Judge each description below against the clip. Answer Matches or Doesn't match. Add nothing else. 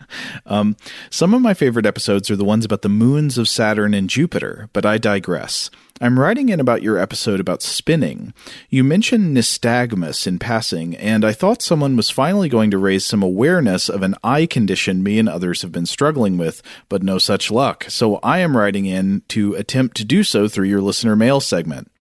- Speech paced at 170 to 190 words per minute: Doesn't match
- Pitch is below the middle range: Matches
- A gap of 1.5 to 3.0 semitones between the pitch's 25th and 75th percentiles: Doesn't match